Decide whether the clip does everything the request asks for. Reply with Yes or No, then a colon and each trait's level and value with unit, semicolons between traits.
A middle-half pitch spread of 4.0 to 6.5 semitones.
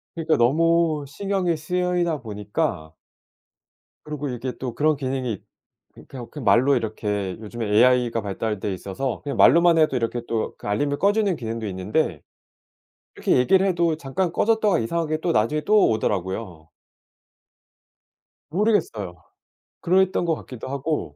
No: wide, 7.2 semitones